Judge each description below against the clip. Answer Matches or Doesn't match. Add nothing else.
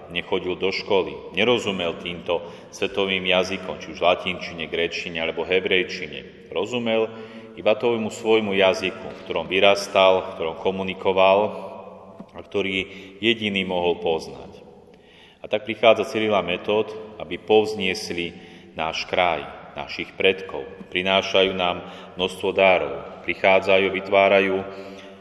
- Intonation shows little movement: Matches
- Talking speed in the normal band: Doesn't match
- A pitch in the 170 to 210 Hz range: Doesn't match